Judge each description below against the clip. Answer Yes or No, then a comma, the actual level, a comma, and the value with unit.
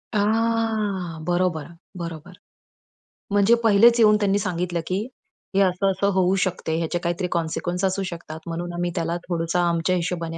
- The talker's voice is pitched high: No, medium, 180 Hz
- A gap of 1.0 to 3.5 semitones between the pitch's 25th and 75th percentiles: Yes, average, 2.8 semitones